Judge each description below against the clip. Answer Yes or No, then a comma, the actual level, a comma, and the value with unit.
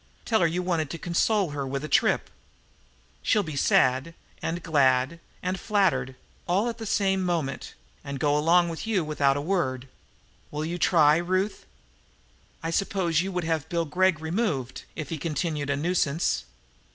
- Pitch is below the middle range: No, medium, 165 Hz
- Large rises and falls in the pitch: No, average, 4.0 semitones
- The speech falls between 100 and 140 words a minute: No, average, 165 wpm